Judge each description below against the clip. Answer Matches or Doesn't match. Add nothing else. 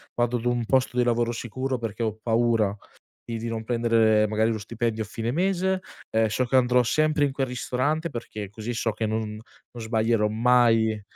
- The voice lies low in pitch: Matches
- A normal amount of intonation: Doesn't match